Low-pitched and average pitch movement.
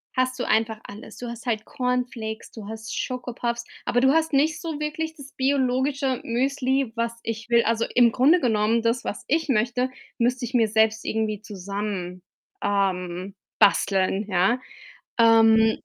No: high, 235 Hz; average, 3.0 semitones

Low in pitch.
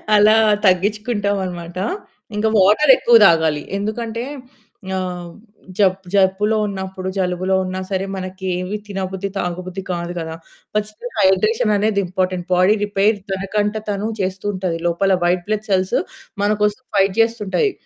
No: high, 195 Hz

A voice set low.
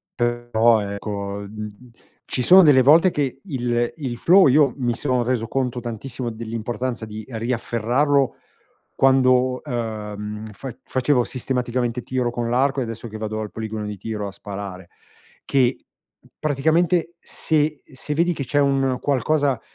Yes: low, 125 Hz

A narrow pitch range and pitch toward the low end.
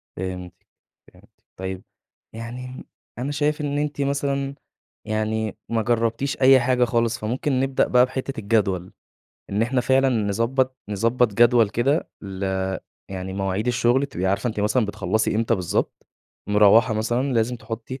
No: average, 3.7 semitones; low, 115 Hz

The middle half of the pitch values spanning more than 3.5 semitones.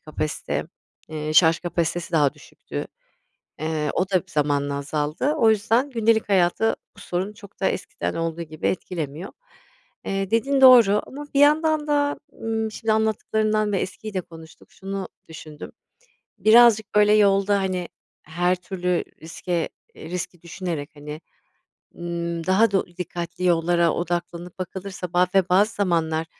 Yes: average, 4.2 semitones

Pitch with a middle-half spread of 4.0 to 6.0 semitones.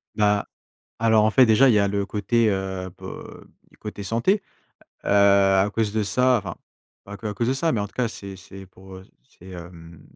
No: average, 2.8 semitones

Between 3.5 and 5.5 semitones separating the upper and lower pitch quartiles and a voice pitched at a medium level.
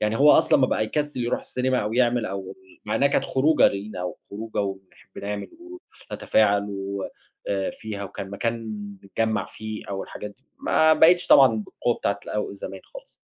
No: average, 3.8 semitones; low, 110 Hz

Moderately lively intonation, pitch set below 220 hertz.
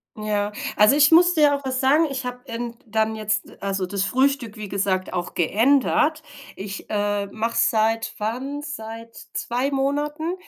No: average, 5.0 semitones; high, 230 Hz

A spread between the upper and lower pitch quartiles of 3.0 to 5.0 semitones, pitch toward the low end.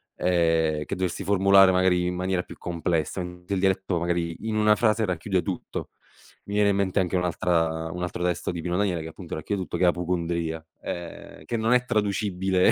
No: narrow, 2.4 semitones; very low, 90 Hz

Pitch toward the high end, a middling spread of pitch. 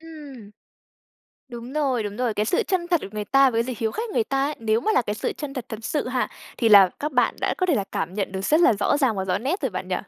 No: high, 245 Hz; wide, 5.8 semitones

